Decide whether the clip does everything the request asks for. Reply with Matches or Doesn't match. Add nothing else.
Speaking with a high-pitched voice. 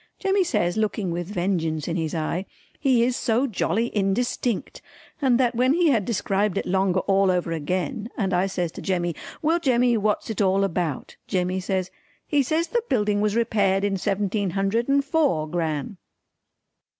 Matches